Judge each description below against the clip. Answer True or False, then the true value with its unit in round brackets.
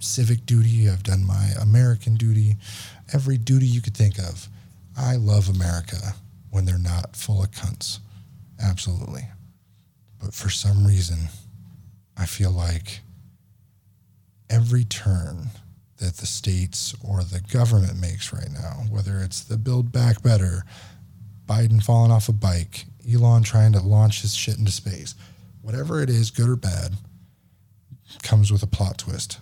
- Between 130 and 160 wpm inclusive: True (145 wpm)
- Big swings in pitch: False (2.9 semitones)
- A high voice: False (105 Hz)